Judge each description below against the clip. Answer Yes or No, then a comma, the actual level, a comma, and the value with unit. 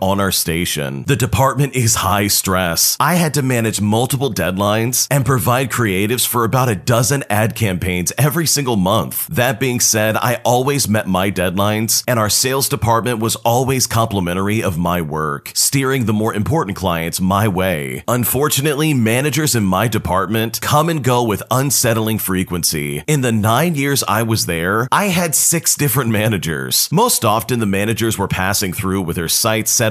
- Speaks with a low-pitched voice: Yes, low, 110 Hz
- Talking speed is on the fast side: No, average, 170 wpm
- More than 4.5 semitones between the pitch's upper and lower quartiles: Yes, average, 5.1 semitones